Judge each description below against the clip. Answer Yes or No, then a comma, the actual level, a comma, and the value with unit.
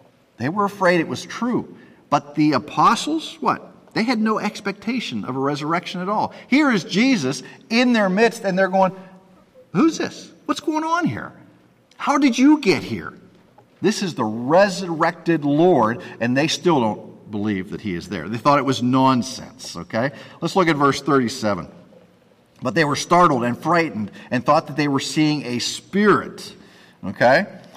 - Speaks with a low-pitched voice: No, medium, 170 Hz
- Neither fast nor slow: Yes, average, 170 wpm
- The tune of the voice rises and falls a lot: Yes, wide, 6.9 semitones